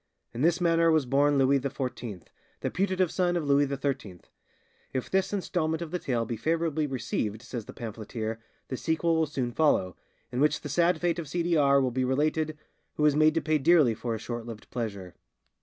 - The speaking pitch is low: No, medium, 145 Hz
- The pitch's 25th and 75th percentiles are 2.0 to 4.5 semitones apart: No, average, 5.1 semitones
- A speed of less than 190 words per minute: No, fast, 205 wpm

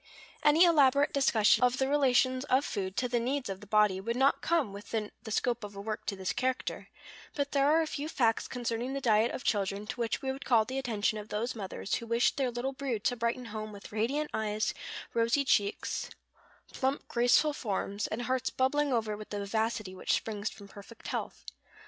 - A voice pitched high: Yes, high, 235 Hz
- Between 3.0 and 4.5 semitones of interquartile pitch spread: Yes, average, 3.9 semitones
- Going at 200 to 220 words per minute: Yes, fast, 205 wpm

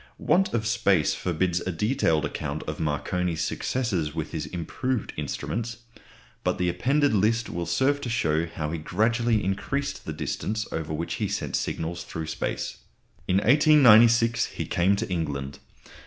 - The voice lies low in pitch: Yes, very low, 95 Hz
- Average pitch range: No, wide, 6.3 semitones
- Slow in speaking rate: No, average, 155 wpm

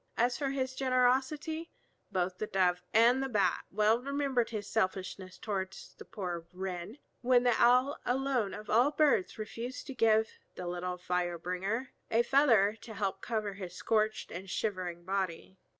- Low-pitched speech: No, high, 215 Hz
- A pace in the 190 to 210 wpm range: No, average, 165 wpm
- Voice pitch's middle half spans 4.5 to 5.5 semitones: Yes, average, 5.2 semitones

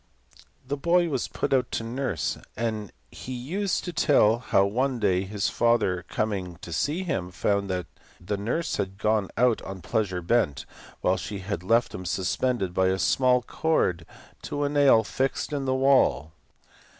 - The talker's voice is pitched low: Yes, low, 110 Hz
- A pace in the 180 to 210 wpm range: No, average, 170 wpm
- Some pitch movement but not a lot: No, wide, 5.8 semitones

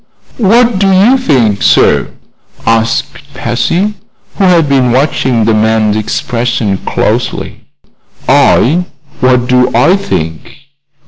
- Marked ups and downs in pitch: Yes, wide, 8.1 semitones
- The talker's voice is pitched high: No, low, 125 Hz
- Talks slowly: Yes, slow, 110 wpm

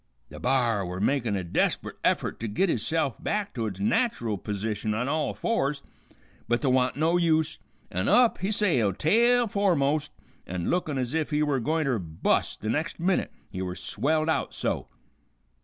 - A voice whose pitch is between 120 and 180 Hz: Yes, medium, 140 Hz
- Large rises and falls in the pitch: Yes, wide, 7.0 semitones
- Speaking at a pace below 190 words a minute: Yes, average, 175 wpm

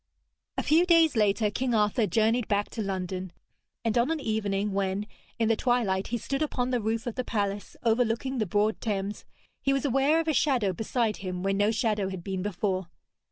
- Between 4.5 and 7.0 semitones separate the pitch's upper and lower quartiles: No, average, 3.8 semitones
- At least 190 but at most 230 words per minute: Yes, average, 200 wpm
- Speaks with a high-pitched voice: Yes, high, 220 Hz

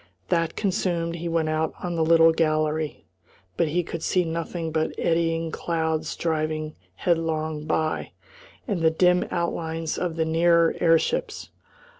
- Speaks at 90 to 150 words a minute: Yes, average, 140 wpm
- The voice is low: No, medium, 165 Hz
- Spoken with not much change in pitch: Yes, narrow, 1.1 semitones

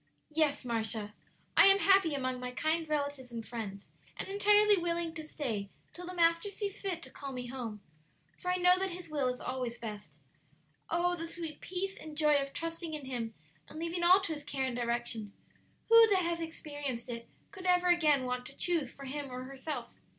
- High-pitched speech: Yes, very high, 300 Hz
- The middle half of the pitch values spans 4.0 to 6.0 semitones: Yes, wide, 5.7 semitones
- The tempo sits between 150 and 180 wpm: No, average, 200 wpm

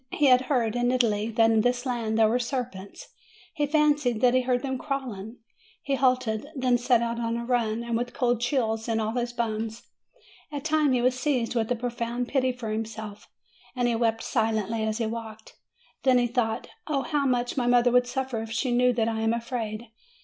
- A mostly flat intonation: Yes, narrow, 2.1 semitones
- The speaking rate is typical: No, fast, 210 wpm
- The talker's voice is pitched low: No, high, 240 Hz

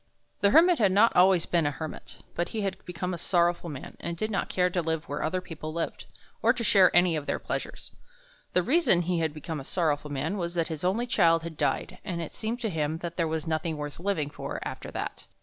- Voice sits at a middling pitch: Yes, medium, 170 Hz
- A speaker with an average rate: No, fast, 235 wpm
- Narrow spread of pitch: No, average, 3.0 semitones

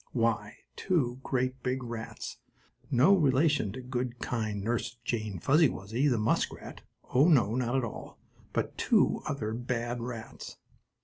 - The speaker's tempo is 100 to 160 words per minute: Yes, slow, 135 wpm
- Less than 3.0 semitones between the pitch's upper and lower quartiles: Yes, narrow, 2.5 semitones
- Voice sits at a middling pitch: No, low, 120 Hz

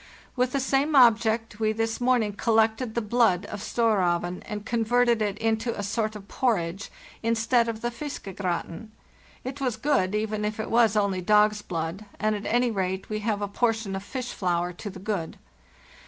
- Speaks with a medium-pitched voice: No, high, 220 Hz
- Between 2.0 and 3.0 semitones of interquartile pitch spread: Yes, average, 2.7 semitones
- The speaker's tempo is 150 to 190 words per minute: Yes, average, 180 wpm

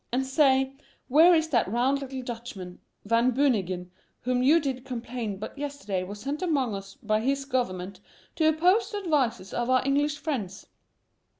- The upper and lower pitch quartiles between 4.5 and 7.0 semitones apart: Yes, average, 4.9 semitones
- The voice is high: Yes, very high, 255 Hz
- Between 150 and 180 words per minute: Yes, average, 165 wpm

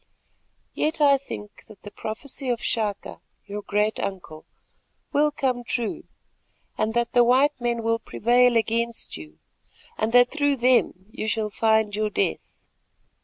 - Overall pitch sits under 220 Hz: No, high, 230 Hz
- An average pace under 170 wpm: Yes, average, 145 wpm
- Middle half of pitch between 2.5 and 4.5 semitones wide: Yes, average, 2.8 semitones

